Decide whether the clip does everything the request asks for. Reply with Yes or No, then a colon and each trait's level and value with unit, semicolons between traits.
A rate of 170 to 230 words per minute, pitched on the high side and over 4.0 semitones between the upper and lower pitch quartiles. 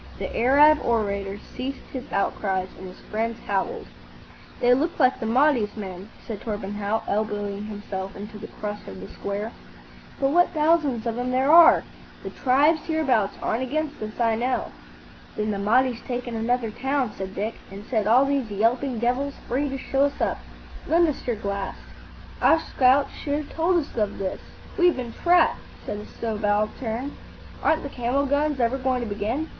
Yes: average, 175 wpm; high, 240 Hz; average, 4.8 semitones